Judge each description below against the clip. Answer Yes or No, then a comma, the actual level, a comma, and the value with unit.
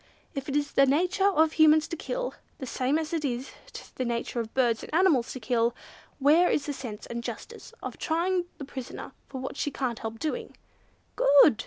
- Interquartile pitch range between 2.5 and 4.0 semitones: No, average, 4.6 semitones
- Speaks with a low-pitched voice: No, very high, 280 Hz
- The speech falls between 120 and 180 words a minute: No, average, 200 wpm